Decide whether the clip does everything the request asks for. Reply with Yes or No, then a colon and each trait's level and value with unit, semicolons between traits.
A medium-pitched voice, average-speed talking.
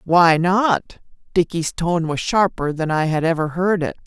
Yes: medium, 170 Hz; average, 175 wpm